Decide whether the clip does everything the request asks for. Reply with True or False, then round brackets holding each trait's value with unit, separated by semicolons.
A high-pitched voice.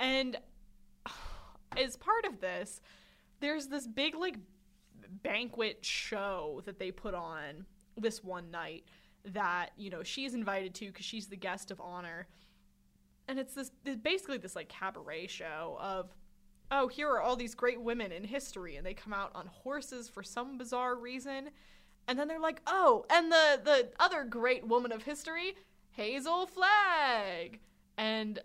True (235 Hz)